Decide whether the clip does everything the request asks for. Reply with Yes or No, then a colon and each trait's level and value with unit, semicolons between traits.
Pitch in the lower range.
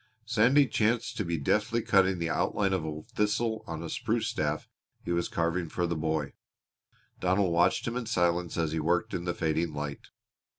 Yes: very low, 85 Hz